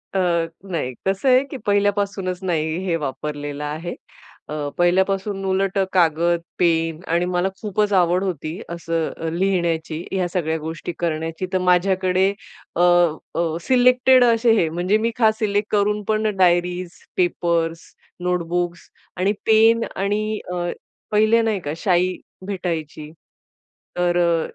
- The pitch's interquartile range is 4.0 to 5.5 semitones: No, average, 3.3 semitones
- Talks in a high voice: No, medium, 180 Hz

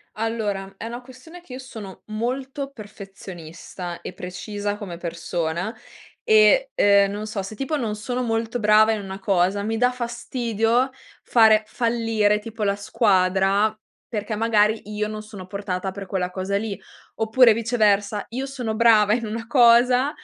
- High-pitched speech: Yes, high, 215 Hz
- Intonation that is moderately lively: Yes, average, 3.0 semitones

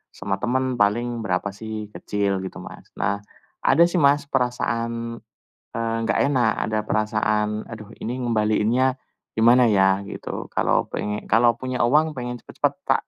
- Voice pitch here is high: No, low, 115 Hz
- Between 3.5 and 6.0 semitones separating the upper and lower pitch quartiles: No, average, 2.8 semitones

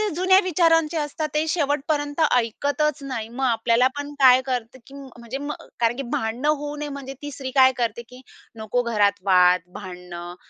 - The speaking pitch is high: Yes, very high, 265 Hz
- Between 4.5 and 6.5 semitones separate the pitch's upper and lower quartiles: No, average, 4.1 semitones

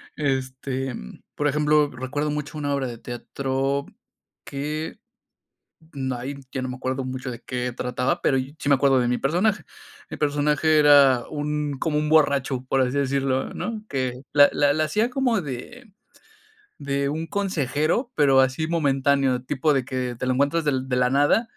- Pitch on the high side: No, medium, 140 Hz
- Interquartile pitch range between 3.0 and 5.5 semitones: No, narrow, 2.5 semitones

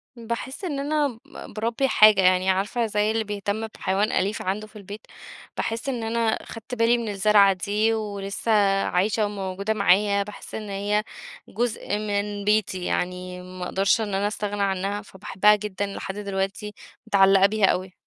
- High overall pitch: Yes, high, 205 Hz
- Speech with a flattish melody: Yes, narrow, 1.9 semitones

